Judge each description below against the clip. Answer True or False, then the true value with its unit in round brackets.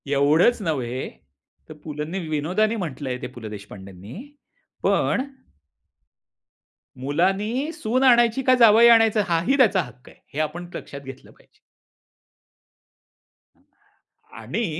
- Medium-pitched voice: True (170 Hz)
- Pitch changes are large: True (8.6 semitones)